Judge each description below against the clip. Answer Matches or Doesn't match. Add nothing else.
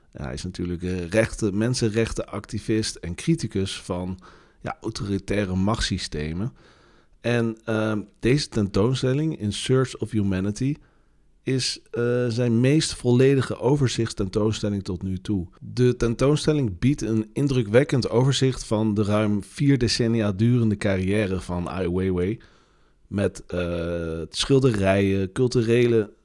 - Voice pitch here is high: Doesn't match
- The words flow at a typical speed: Doesn't match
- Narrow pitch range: Doesn't match